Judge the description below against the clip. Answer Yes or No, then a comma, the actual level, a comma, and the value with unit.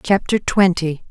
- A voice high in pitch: No, medium, 180 Hz